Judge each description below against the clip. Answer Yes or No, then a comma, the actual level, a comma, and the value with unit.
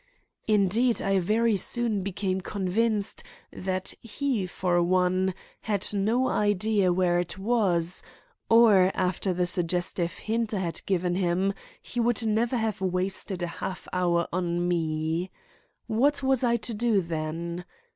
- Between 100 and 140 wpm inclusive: Yes, slow, 135 wpm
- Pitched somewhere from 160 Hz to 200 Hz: Yes, high, 190 Hz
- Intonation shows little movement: No, average, 3.7 semitones